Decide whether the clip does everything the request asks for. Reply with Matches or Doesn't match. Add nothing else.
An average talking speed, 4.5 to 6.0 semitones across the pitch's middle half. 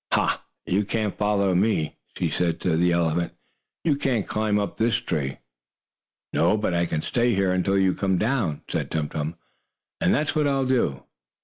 Matches